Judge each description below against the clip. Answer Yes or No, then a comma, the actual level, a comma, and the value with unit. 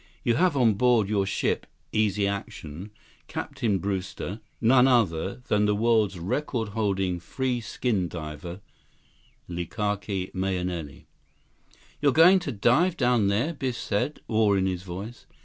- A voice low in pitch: Yes, low, 105 Hz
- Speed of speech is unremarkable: No, slow, 130 wpm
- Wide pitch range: No, average, 4.4 semitones